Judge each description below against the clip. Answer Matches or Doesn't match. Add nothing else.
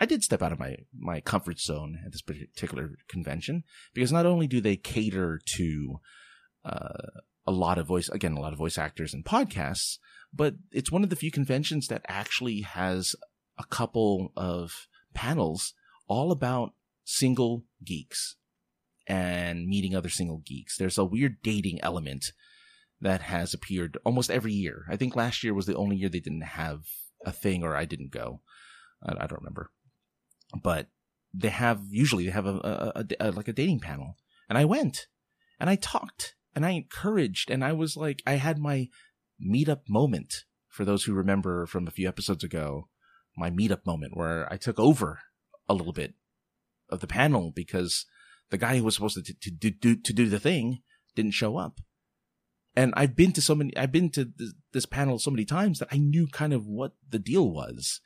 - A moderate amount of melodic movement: Doesn't match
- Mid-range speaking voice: Doesn't match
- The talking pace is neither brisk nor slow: Matches